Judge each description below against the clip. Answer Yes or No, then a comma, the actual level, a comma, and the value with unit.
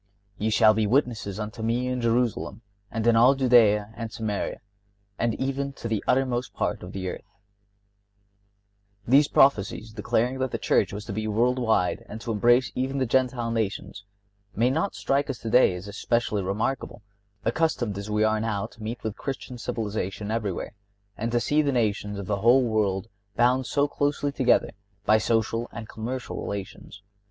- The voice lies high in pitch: No, low, 115 Hz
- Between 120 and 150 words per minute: No, average, 170 wpm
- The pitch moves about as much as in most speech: Yes, average, 3.1 semitones